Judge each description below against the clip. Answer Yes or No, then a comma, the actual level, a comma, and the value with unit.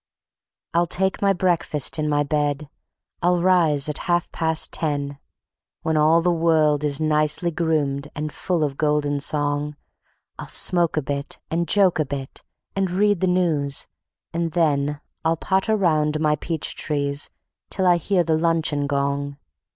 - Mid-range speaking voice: Yes, medium, 155 Hz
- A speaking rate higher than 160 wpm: No, average, 155 wpm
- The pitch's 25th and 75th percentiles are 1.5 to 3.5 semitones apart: Yes, average, 2.9 semitones